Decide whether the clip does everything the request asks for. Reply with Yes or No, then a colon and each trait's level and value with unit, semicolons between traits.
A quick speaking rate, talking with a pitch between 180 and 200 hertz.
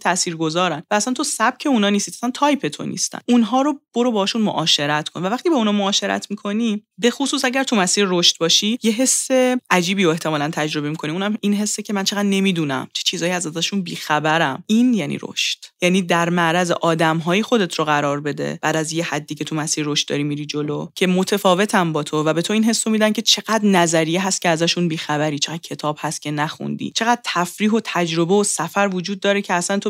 Yes: fast, 215 wpm; medium, 185 Hz